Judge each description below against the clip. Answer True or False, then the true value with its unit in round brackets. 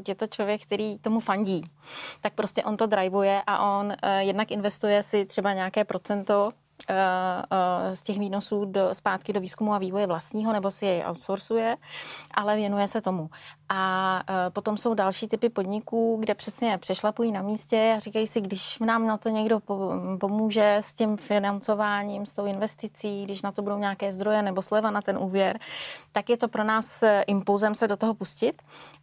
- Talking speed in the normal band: False (180 wpm)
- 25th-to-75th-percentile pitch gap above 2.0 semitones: False (1.7 semitones)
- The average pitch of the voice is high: True (205 Hz)